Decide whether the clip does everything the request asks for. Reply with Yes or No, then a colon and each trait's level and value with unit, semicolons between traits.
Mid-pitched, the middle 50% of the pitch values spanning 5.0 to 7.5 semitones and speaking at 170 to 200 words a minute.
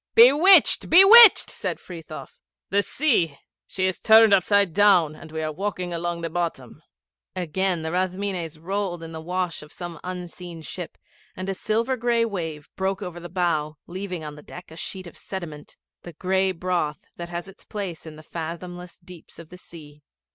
No: medium, 180 Hz; average, 2.9 semitones; average, 175 wpm